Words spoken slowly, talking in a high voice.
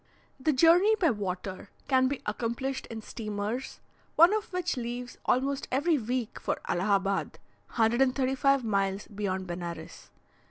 Yes: slow, 125 wpm; high, 245 Hz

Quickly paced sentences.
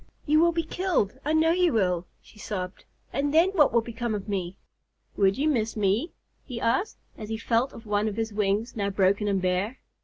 Yes: fast, 210 wpm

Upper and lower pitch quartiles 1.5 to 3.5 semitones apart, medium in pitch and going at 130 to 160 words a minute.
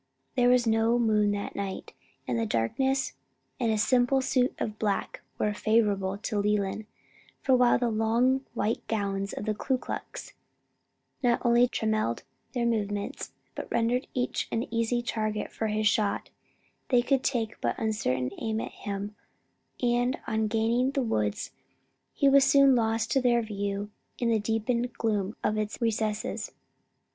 No: average, 2.7 semitones; high, 225 Hz; average, 155 wpm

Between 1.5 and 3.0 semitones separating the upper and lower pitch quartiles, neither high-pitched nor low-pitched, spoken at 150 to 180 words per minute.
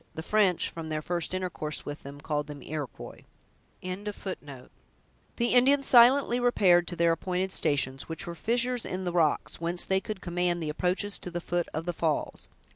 No: average, 3.9 semitones; medium, 175 Hz; average, 175 wpm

